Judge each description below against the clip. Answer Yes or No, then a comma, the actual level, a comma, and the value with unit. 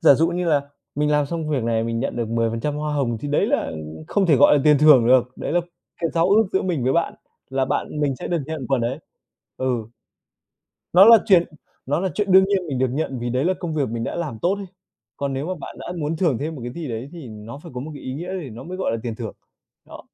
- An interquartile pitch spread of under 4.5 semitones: No, average, 5.2 semitones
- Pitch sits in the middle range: Yes, medium, 145 Hz